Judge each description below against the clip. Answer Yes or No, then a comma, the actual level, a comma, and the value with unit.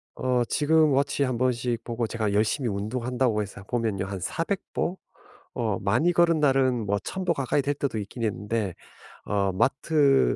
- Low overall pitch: Yes, low, 120 Hz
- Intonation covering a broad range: No, average, 5.0 semitones